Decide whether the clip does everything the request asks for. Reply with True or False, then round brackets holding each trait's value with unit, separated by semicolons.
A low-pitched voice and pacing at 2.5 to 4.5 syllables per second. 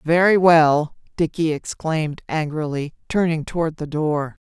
False (160 Hz; 4.3 syllables/s)